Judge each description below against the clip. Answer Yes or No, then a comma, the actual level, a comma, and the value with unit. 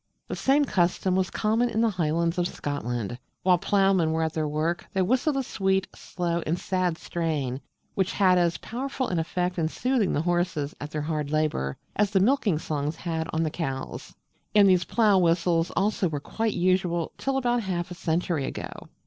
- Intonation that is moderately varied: Yes, average, 3.6 semitones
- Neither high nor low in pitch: Yes, medium, 175 Hz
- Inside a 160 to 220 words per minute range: Yes, average, 190 wpm